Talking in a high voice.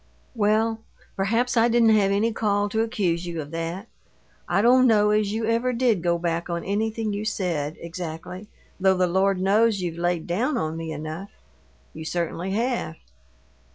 Yes: high, 200 Hz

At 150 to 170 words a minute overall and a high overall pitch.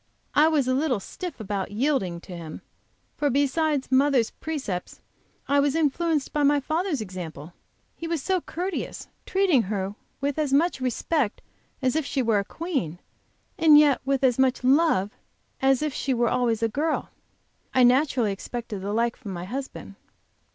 Yes: average, 165 wpm; very high, 265 Hz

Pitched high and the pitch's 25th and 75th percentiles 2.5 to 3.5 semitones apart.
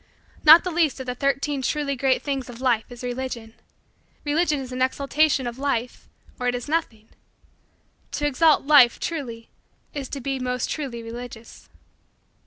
Yes: very high, 260 Hz; average, 3.0 semitones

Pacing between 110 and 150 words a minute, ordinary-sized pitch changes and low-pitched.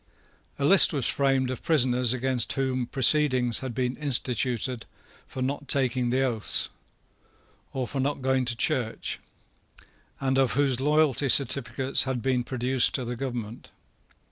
No: average, 140 wpm; narrow, 1.7 semitones; low, 130 Hz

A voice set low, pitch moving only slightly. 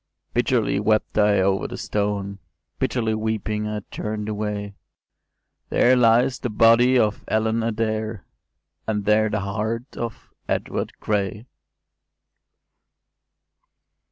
Yes: low, 110 Hz; narrow, 1.5 semitones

